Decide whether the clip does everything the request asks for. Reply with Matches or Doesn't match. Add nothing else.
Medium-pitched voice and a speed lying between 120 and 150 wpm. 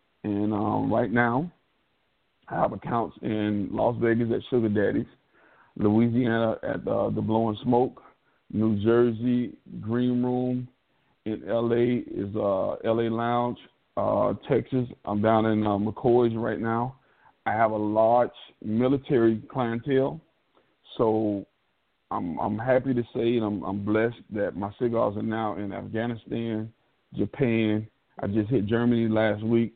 Doesn't match